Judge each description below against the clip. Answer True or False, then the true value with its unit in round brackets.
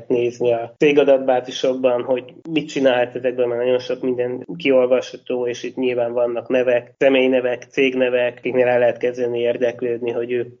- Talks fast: False (145 wpm)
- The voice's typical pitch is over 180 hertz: False (125 Hz)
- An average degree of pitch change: False (1.0 semitones)